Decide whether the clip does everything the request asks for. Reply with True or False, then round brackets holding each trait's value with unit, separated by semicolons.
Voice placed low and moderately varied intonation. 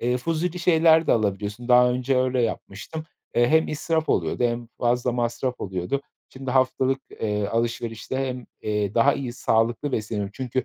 True (125 Hz; 3.0 semitones)